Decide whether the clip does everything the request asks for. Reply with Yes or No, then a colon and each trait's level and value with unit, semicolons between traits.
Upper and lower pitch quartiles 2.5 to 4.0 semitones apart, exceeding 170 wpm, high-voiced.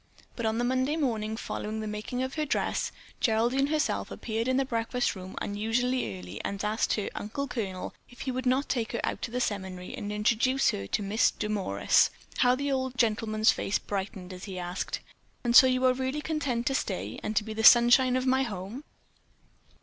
Yes: average, 3.6 semitones; average, 195 wpm; high, 230 Hz